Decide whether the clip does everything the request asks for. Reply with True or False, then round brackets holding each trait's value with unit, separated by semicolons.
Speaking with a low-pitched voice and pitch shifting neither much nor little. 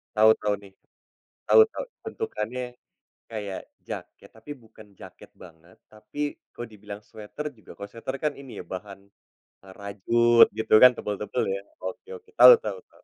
True (105 Hz; 3.0 semitones)